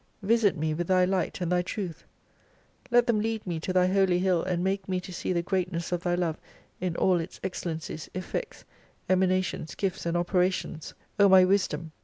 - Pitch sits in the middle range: Yes, medium, 180 Hz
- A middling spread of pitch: No, narrow, 1.6 semitones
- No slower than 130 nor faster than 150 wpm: No, average, 195 wpm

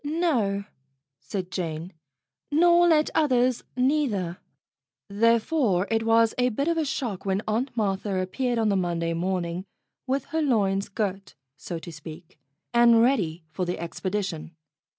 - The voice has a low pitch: No, high, 210 Hz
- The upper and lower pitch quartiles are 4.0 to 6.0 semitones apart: Yes, wide, 5.6 semitones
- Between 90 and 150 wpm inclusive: Yes, average, 140 wpm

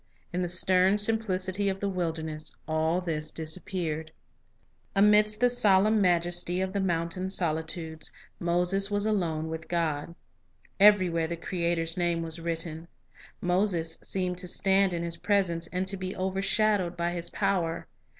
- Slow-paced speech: No, average, 150 wpm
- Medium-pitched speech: Yes, medium, 180 Hz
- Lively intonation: No, average, 2.7 semitones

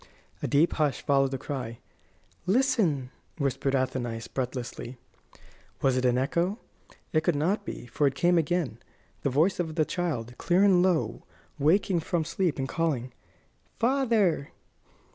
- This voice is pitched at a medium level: Yes, medium, 150 Hz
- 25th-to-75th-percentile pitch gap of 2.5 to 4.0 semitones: No, average, 5.1 semitones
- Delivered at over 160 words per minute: No, average, 145 wpm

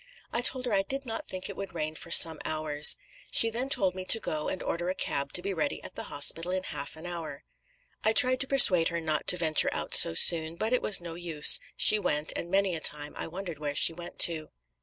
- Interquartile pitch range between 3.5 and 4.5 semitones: Yes, average, 4.0 semitones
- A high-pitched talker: No, medium, 175 Hz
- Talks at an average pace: No, fast, 245 wpm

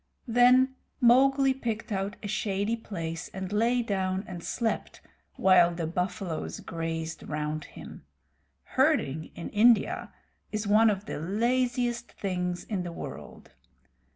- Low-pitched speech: No, high, 200 Hz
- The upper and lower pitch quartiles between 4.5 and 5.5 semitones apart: Yes, average, 5.1 semitones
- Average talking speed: No, slow, 125 wpm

